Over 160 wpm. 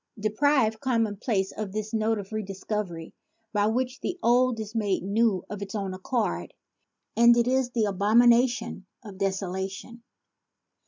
No: average, 150 wpm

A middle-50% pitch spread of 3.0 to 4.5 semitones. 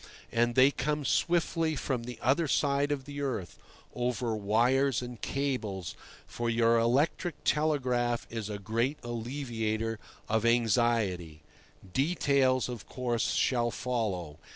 Yes: average, 3.5 semitones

